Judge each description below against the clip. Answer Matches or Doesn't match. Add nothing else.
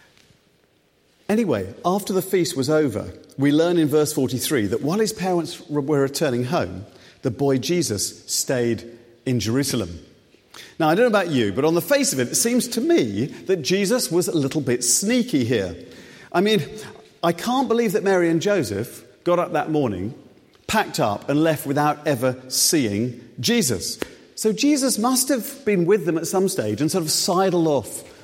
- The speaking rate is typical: Matches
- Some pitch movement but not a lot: Doesn't match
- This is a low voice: Doesn't match